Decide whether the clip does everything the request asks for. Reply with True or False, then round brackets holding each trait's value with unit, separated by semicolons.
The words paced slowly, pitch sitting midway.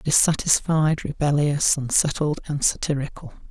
True (85 wpm; 145 Hz)